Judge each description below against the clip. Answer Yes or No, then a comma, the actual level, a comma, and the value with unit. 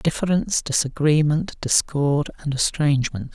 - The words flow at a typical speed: No, slow, 90 wpm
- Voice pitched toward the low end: No, medium, 150 Hz